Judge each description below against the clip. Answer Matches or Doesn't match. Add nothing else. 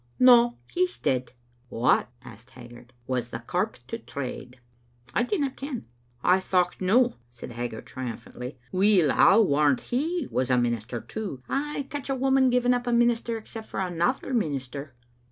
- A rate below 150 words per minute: Doesn't match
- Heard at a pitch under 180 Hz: Doesn't match